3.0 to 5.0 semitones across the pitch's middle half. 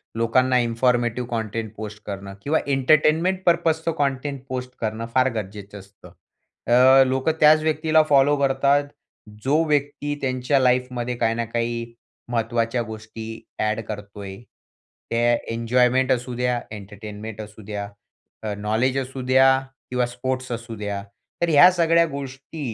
Yes: average, 3.6 semitones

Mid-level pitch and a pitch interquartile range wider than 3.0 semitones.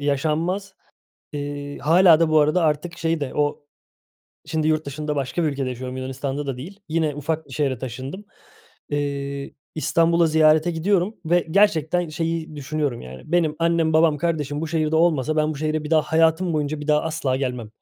No: medium, 155 Hz; narrow, 2.4 semitones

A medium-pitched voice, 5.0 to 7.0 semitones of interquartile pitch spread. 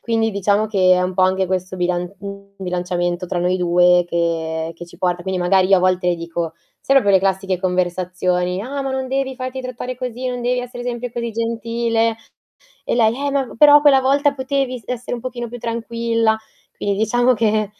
No: high, 215 Hz; wide, 5.4 semitones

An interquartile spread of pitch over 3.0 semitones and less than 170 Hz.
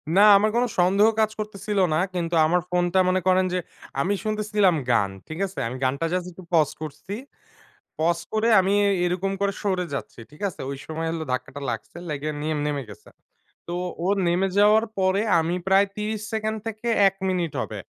No: average, 3.9 semitones; medium, 185 Hz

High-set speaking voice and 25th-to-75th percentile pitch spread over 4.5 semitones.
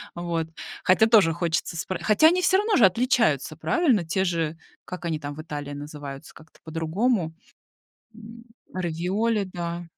No: medium, 175 Hz; wide, 5.6 semitones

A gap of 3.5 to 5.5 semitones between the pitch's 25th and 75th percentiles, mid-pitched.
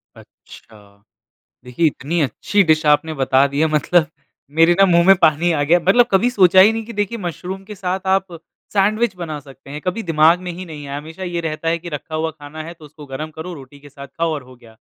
Yes: average, 3.9 semitones; medium, 160 Hz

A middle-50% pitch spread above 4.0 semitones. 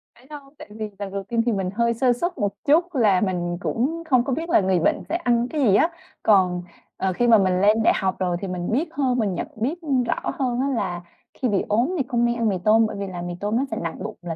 Yes: average, 5.2 semitones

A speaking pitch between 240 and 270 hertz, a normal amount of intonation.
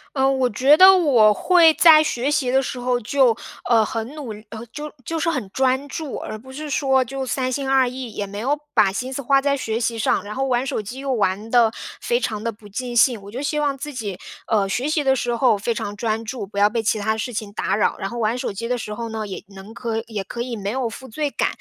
Yes: high, 245 Hz; average, 3.7 semitones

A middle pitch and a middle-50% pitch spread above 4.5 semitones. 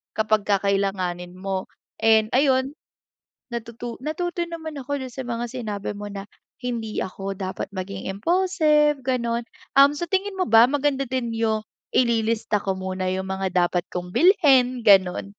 No: high, 230 Hz; wide, 5.5 semitones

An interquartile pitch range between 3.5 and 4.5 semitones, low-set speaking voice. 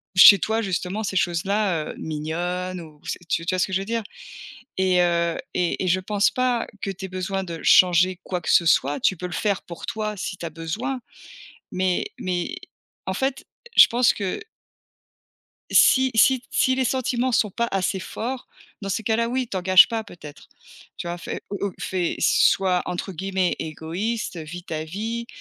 No: average, 4.0 semitones; high, 190 Hz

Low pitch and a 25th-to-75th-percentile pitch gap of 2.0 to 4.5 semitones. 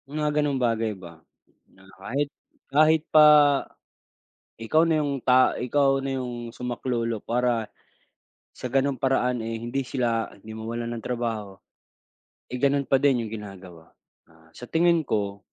Yes: low, 125 Hz; average, 3.7 semitones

